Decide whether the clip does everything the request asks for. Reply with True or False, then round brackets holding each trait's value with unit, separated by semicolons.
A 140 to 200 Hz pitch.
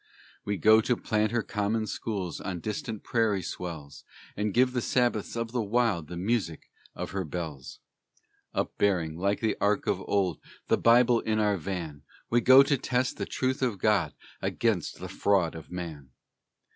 False (105 Hz)